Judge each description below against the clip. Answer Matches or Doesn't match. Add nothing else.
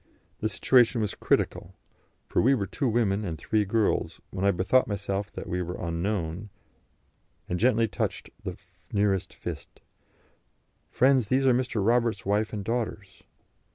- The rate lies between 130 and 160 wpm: Matches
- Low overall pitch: Matches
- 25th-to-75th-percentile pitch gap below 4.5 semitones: Matches